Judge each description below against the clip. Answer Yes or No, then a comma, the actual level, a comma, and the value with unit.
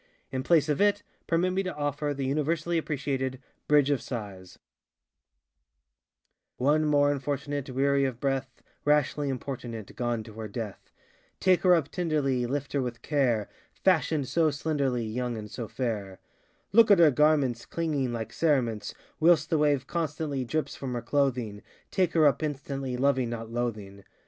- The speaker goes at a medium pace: Yes, average, 155 wpm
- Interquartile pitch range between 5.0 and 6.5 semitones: No, average, 3.9 semitones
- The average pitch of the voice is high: No, medium, 140 Hz